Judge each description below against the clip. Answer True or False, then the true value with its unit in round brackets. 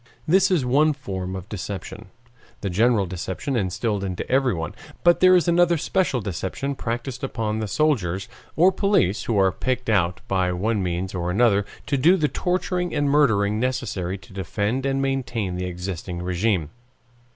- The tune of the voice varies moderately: False (6.6 semitones)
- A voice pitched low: True (110 Hz)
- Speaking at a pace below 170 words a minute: True (160 wpm)